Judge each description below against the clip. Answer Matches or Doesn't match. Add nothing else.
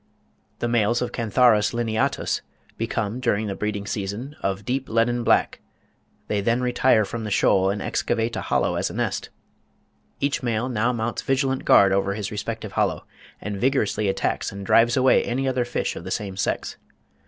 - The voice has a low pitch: Matches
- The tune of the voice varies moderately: Matches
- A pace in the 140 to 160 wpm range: Doesn't match